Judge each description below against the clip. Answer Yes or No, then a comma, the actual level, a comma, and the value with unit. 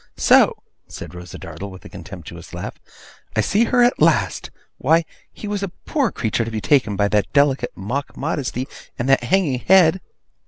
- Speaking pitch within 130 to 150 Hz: Yes, low, 135 Hz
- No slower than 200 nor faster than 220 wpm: No, average, 180 wpm